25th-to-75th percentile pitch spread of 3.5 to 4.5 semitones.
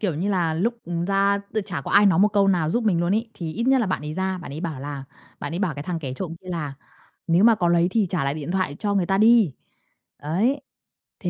Yes: average, 3.9 semitones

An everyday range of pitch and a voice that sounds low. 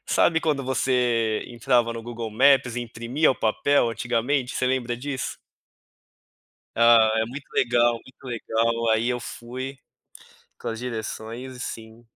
No: narrow, 2.1 semitones; low, 120 Hz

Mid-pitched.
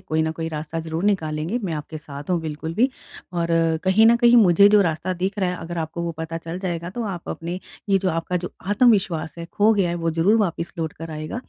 Yes: medium, 170 Hz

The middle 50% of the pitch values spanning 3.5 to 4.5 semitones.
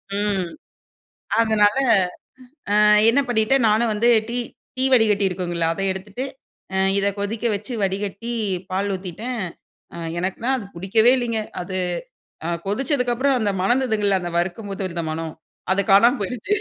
Yes: average, 3.8 semitones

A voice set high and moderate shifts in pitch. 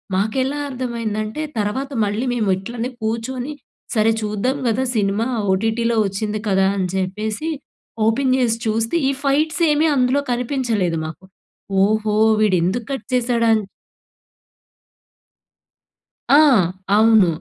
Yes: high, 225 Hz; average, 3.2 semitones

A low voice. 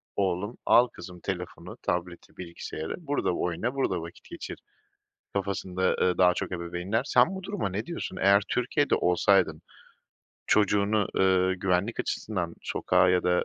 Yes: very low, 95 Hz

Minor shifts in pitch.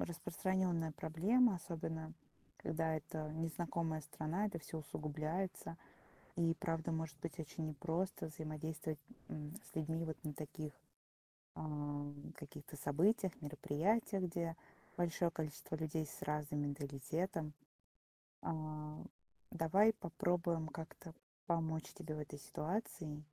Yes: narrow, 1.8 semitones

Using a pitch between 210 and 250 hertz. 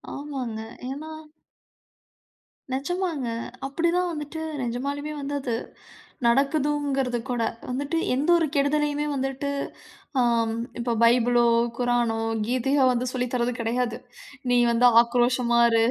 No: very high, 260 Hz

